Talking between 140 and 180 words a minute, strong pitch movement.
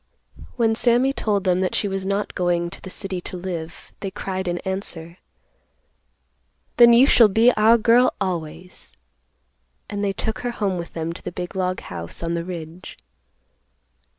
No: average, 170 wpm; average, 3.6 semitones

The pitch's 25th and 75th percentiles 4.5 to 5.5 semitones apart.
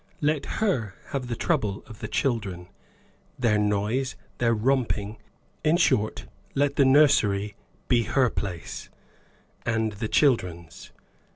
Yes: average, 4.8 semitones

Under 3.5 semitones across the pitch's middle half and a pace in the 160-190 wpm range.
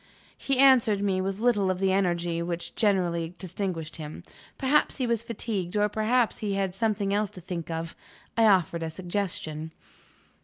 No: average, 3.9 semitones; average, 165 wpm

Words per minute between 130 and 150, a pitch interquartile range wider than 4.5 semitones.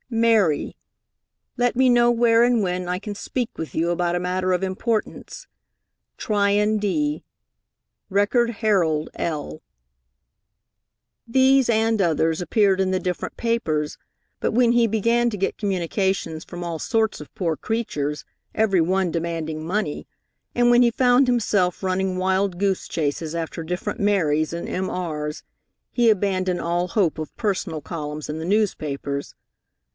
Yes: average, 140 wpm; average, 5.0 semitones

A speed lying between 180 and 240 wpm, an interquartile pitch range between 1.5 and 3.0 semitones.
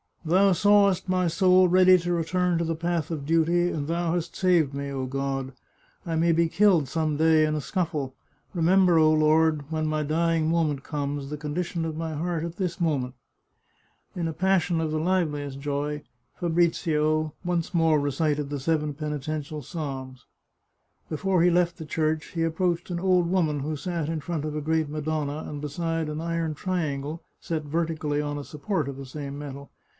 Yes: average, 185 wpm; narrow, 2.5 semitones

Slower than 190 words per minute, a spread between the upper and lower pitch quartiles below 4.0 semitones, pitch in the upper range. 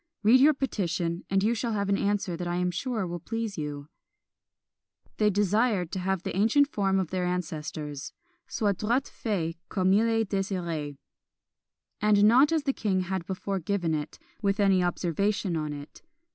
Yes: average, 175 wpm; average, 3.5 semitones; high, 195 Hz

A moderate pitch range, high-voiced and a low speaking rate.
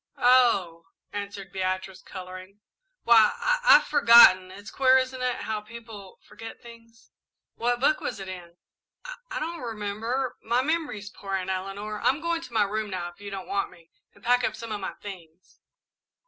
No: average, 4.3 semitones; high, 210 Hz; average, 180 wpm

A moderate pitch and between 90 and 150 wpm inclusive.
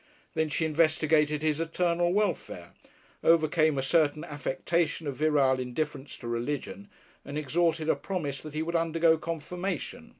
Yes: medium, 155 Hz; average, 140 wpm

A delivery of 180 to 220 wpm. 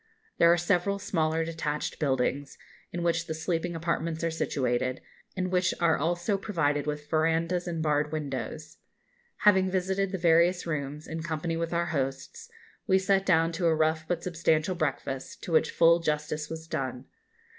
No: average, 165 wpm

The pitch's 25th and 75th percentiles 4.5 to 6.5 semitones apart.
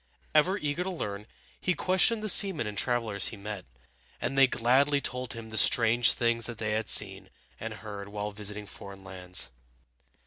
Yes: average, 5.1 semitones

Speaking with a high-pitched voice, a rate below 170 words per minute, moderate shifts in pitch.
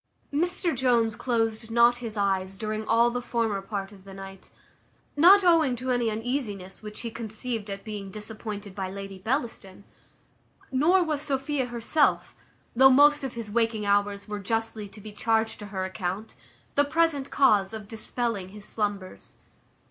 Yes: high, 225 Hz; average, 160 wpm; average, 3.8 semitones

